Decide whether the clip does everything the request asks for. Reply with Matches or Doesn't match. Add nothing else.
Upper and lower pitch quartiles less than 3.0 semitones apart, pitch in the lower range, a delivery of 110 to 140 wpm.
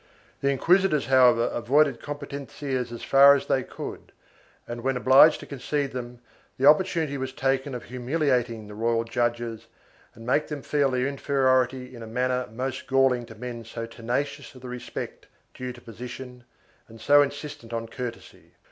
Doesn't match